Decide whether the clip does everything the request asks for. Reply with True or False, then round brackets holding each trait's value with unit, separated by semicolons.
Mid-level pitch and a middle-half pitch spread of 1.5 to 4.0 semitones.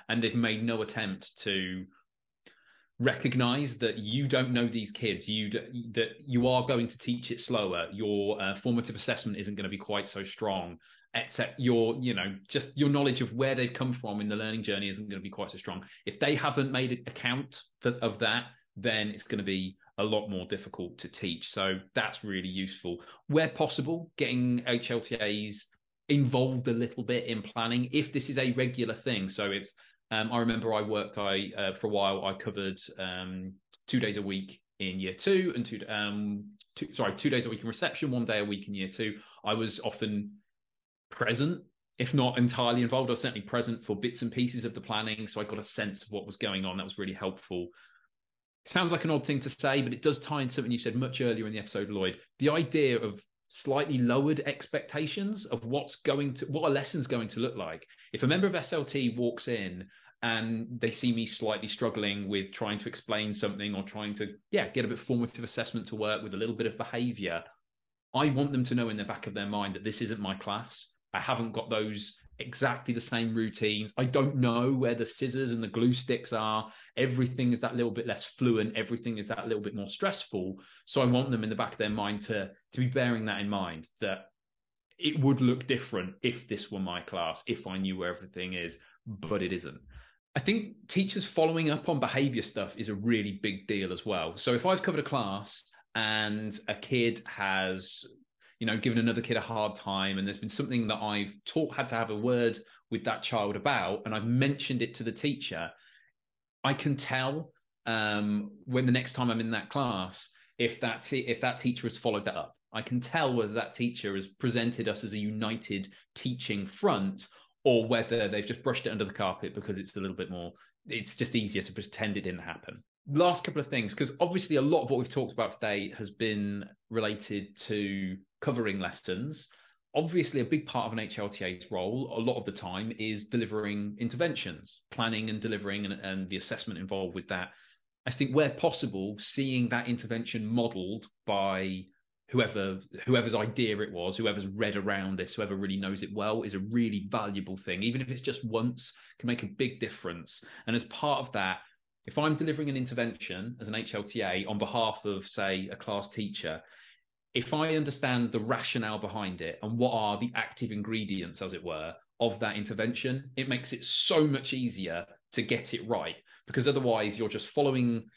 False (115 Hz; 3.5 semitones)